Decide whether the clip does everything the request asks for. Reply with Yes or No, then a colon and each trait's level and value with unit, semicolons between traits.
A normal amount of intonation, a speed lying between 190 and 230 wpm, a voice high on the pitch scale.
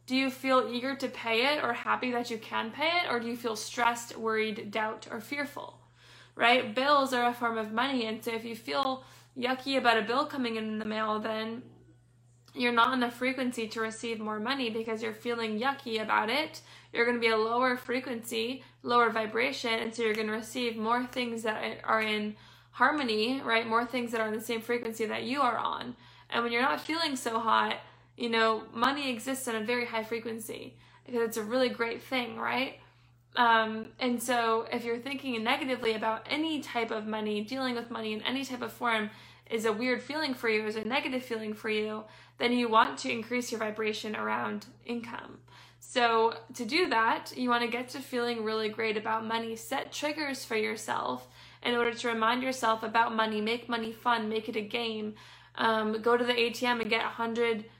No: narrow, 1.9 semitones; fast, 205 wpm; high, 235 Hz